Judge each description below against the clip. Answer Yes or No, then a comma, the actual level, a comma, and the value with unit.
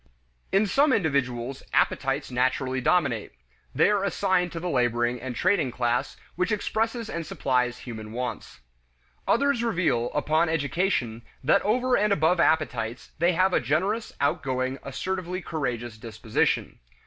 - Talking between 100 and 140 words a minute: Yes, slow, 135 wpm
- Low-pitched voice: No, medium, 150 Hz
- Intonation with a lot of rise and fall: Yes, wide, 7.1 semitones